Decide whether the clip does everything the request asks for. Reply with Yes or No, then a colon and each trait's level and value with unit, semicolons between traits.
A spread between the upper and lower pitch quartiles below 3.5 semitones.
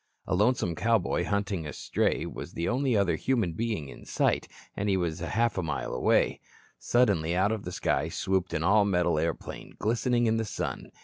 No: average, 4.7 semitones